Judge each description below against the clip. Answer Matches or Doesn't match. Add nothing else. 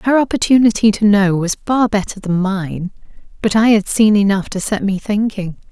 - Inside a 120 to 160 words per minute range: Doesn't match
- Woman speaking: Matches